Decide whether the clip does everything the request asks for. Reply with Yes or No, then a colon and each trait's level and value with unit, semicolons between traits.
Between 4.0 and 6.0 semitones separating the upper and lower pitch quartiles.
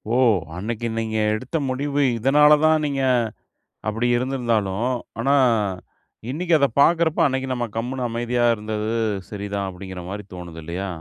Yes: average, 4.7 semitones